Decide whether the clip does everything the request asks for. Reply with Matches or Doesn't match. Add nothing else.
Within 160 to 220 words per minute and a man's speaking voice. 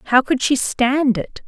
Doesn't match